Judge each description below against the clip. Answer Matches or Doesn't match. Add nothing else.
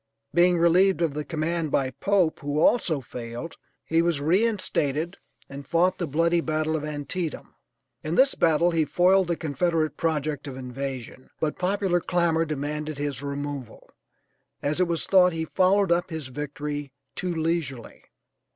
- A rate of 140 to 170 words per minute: Matches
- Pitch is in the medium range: Matches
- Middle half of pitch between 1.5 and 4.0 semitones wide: Matches